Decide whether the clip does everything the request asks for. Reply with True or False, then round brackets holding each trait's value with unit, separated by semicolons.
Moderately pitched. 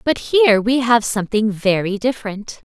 False (225 Hz)